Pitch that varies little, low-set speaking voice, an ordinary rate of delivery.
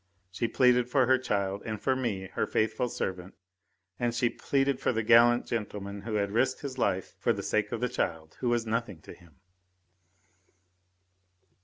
No: average, 3.6 semitones; low, 115 Hz; average, 175 wpm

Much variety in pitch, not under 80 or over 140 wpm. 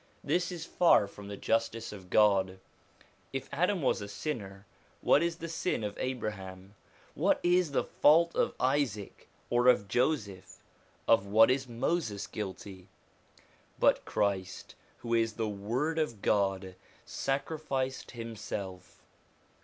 Yes: wide, 6.0 semitones; slow, 135 wpm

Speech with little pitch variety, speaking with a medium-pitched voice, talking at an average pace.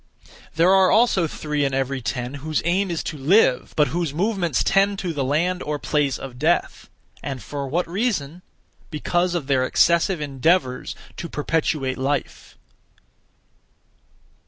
No: average, 4.5 semitones; medium, 155 Hz; average, 145 wpm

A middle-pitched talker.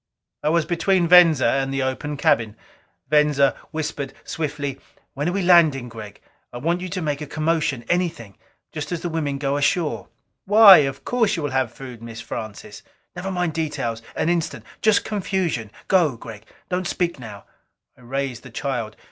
Yes: medium, 150 Hz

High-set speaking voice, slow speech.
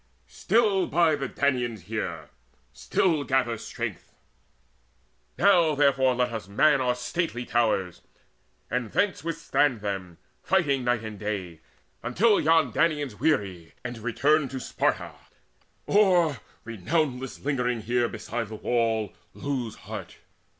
No: low, 125 Hz; slow, 120 wpm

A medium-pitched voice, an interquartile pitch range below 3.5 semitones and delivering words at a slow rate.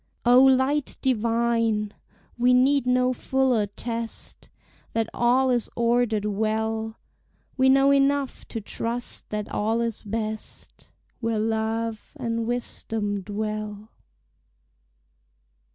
No: high, 230 Hz; narrow, 2.5 semitones; slow, 105 wpm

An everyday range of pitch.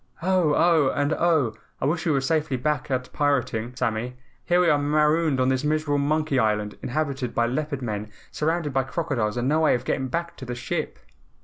Yes: average, 3.7 semitones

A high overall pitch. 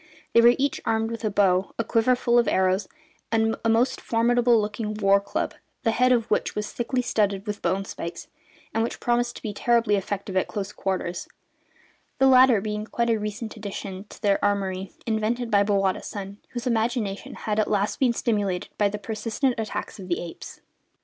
Yes: high, 215 Hz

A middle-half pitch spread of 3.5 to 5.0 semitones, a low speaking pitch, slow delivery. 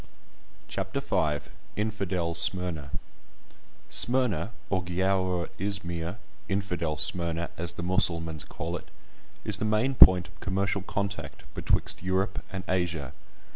No: average, 2.7 semitones; very low, 90 Hz; slow, 110 wpm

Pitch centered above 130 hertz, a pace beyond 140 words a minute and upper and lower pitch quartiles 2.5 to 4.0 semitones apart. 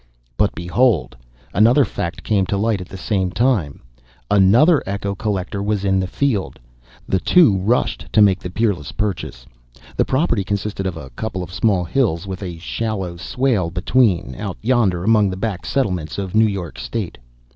No: low, 100 Hz; average, 170 wpm; average, 3.5 semitones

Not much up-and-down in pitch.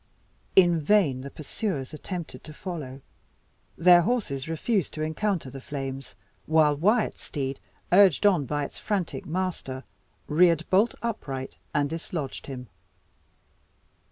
No: average, 5.2 semitones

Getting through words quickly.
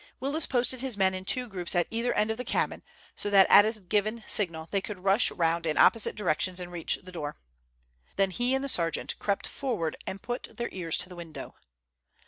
Yes: fast, 215 wpm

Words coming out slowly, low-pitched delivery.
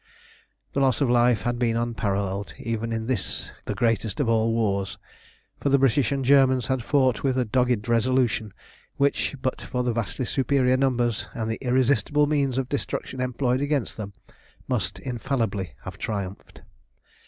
No: average, 160 wpm; low, 125 Hz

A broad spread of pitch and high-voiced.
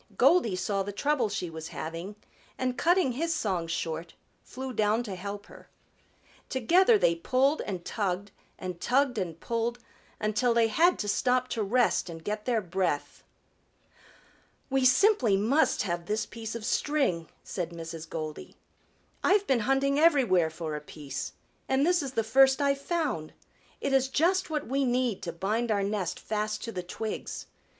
Yes: wide, 6.6 semitones; high, 220 Hz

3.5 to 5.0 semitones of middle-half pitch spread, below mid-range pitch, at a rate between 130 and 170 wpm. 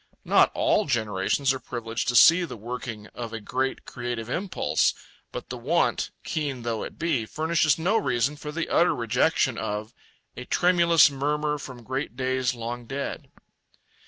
Yes: average, 4.2 semitones; low, 130 Hz; average, 160 wpm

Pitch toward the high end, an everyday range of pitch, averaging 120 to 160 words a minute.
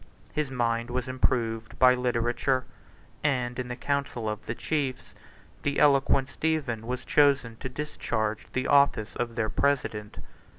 No: low, 125 Hz; average, 3.2 semitones; average, 145 wpm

